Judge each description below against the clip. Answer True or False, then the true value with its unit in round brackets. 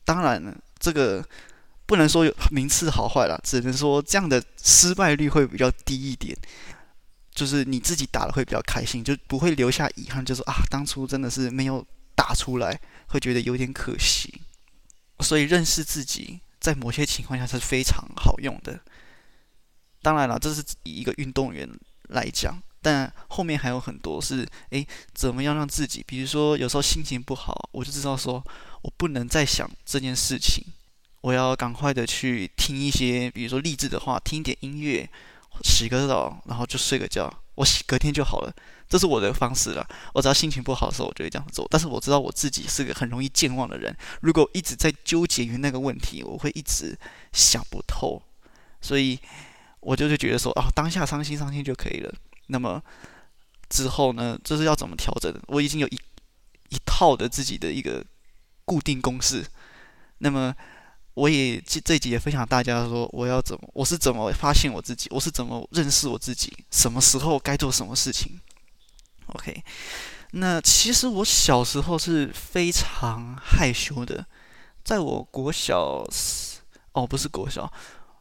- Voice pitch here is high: False (135 Hz)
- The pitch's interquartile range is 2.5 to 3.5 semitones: True (2.8 semitones)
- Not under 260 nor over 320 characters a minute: True (270 characters per minute)